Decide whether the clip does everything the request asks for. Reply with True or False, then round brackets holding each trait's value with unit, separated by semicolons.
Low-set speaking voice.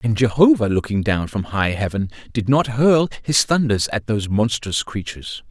True (115 Hz)